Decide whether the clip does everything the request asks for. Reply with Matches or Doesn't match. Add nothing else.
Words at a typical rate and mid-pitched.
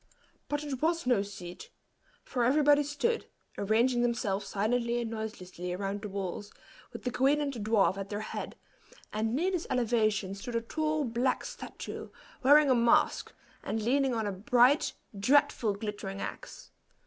Doesn't match